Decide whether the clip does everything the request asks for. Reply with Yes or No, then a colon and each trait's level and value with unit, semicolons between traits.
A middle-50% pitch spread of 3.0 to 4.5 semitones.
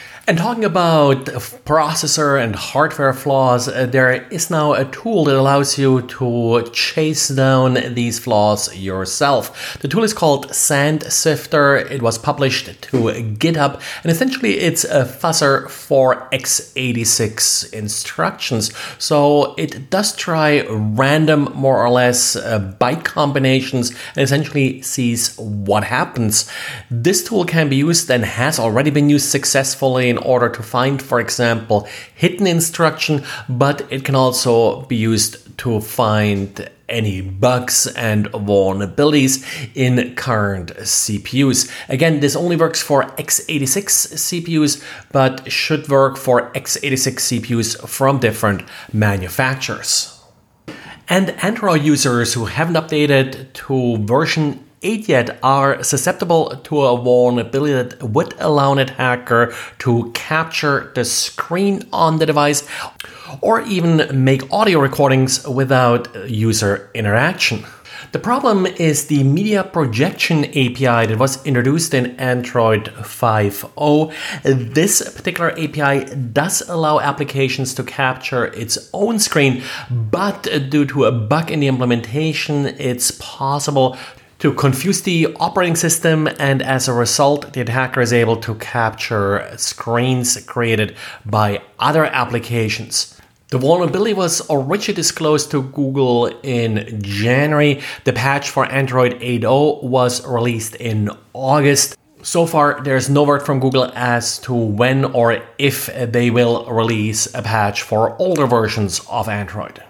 Yes: average, 3.9 semitones